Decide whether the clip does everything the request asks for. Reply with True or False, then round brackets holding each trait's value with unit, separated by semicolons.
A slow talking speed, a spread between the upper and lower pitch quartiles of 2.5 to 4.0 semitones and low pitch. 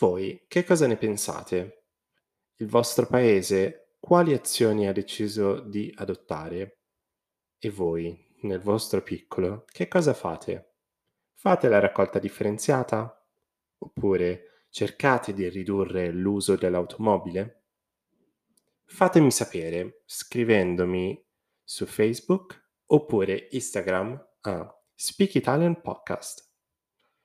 False (95 wpm; 5.0 semitones; 105 Hz)